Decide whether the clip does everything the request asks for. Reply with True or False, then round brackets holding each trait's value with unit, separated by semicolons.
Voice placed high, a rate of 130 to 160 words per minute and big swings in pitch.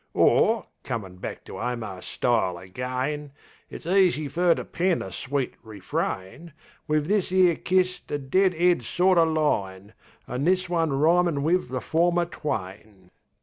False (150 Hz; 145 wpm; 7.0 semitones)